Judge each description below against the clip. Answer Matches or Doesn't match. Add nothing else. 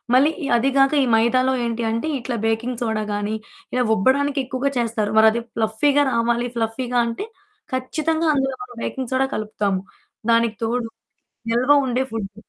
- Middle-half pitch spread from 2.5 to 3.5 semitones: Matches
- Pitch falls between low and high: Doesn't match